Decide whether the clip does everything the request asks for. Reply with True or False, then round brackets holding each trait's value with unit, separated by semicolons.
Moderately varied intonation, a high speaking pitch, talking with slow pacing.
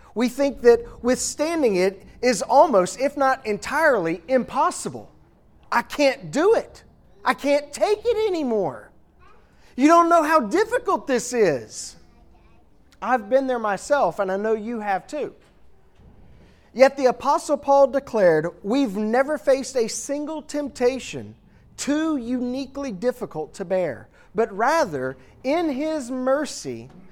False (6.4 semitones; 250 Hz; 130 wpm)